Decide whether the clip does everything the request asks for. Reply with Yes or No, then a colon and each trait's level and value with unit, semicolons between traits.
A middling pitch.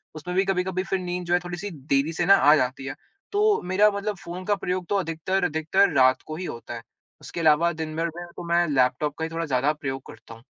Yes: medium, 165 Hz